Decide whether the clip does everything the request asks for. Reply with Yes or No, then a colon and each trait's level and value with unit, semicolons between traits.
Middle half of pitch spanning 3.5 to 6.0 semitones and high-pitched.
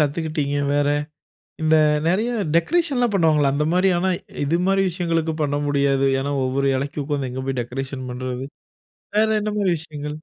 No: average, 4.3 semitones; medium, 150 Hz